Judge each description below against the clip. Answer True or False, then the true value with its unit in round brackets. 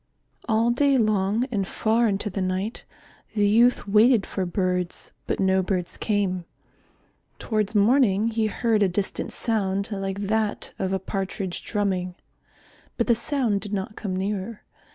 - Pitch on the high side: True (205 Hz)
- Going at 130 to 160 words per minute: True (150 wpm)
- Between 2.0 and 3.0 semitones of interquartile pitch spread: True (2.6 semitones)